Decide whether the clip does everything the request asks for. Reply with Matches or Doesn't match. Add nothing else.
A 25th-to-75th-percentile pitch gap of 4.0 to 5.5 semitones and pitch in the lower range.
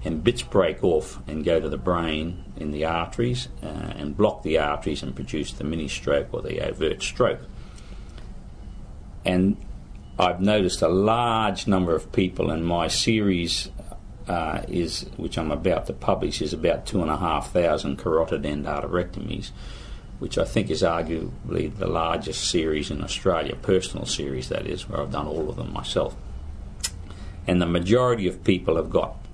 Matches